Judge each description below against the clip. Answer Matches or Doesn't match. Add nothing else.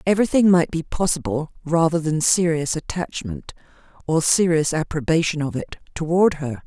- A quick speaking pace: Doesn't match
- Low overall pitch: Doesn't match